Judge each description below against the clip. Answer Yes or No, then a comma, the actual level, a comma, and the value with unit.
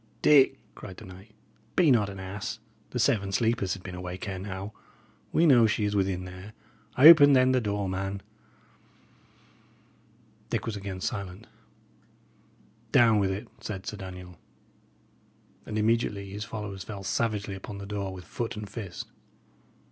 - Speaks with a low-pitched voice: Yes, low, 100 Hz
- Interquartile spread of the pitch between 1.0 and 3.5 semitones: Yes, average, 2.9 semitones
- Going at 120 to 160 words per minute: Yes, average, 150 wpm